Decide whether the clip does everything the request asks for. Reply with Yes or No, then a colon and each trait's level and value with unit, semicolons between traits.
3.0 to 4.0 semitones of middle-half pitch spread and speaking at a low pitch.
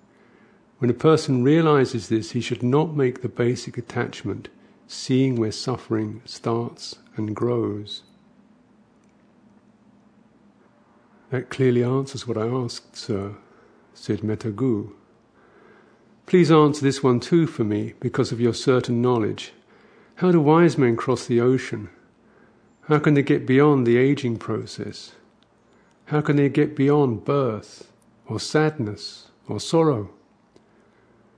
No: average, 4.7 semitones; low, 130 Hz